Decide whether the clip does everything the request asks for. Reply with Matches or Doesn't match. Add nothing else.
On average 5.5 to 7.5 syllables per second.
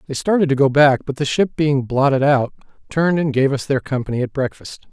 Matches